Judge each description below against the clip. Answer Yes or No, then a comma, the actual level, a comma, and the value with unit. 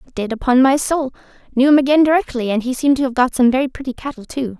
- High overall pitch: Yes, very high, 260 Hz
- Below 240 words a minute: No, fast, 250 wpm